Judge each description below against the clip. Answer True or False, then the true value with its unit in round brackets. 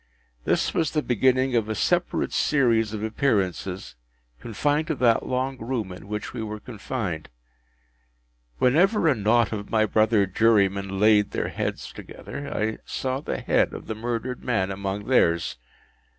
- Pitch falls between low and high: False (110 Hz)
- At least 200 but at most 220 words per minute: False (150 wpm)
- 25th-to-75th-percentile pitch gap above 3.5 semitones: True (4.0 semitones)